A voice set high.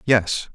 No: low, 110 Hz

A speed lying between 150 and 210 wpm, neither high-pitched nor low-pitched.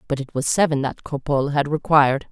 Yes: fast, 205 wpm; medium, 145 Hz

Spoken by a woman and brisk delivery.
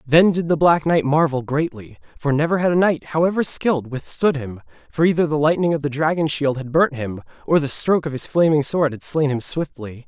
No: male; fast, 225 wpm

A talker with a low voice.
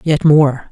No: medium, 145 Hz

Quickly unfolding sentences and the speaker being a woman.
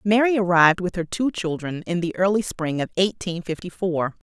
No: average, 195 wpm; female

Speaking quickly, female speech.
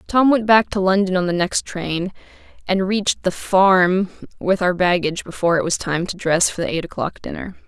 Yes: fast, 210 wpm; female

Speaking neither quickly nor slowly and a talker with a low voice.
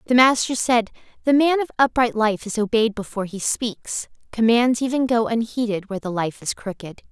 No: average, 185 wpm; high, 230 Hz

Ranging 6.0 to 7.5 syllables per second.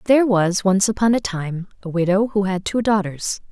No: 5.1 syllables/s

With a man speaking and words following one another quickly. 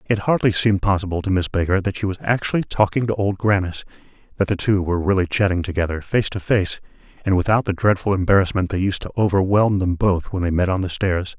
Yes: male; fast, 220 wpm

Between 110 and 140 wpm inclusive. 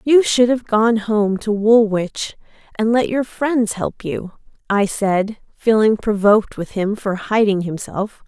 No: average, 160 wpm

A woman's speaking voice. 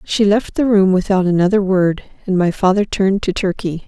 Yes: female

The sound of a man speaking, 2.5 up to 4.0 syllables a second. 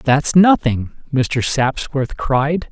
Yes: male; 2.9 syllables/s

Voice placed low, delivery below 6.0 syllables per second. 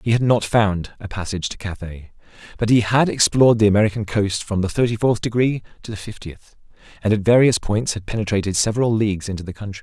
No: low, 105 Hz; 6.3 syllables/s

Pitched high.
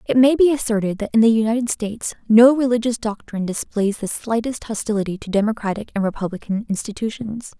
Yes: high, 220 Hz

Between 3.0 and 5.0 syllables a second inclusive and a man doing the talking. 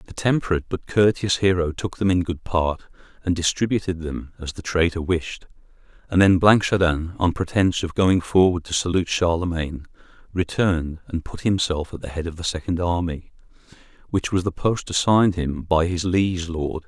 No: 5.3 syllables/s; male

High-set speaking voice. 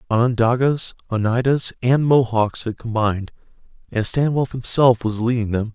No: low, 120 Hz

